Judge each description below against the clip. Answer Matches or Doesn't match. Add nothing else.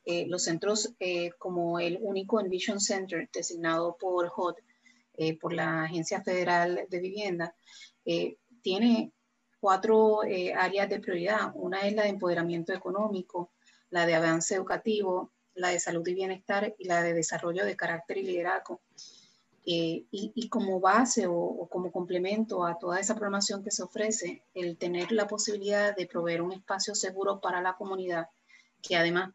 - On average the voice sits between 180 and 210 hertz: Matches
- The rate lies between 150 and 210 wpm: Matches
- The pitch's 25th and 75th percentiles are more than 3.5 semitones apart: Doesn't match